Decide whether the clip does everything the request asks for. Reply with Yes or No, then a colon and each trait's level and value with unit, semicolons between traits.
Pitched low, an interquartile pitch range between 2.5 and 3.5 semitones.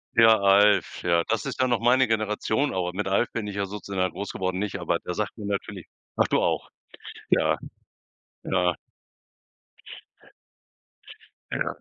Yes: low, 100 Hz; average, 2.9 semitones